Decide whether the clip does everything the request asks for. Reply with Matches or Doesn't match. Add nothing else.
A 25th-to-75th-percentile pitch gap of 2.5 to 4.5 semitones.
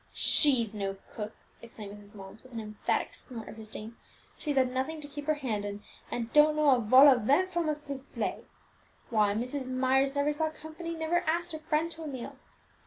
Doesn't match